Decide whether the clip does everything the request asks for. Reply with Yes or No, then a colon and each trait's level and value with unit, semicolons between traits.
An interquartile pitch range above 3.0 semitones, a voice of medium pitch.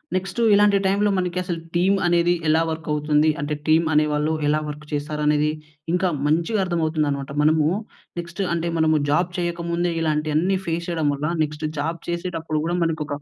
No: narrow, 2.4 semitones; medium, 160 Hz